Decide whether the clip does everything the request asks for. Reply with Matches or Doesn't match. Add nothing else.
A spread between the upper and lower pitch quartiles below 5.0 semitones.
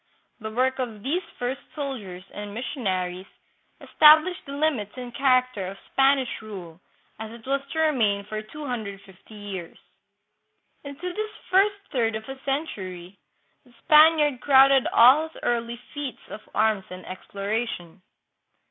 Doesn't match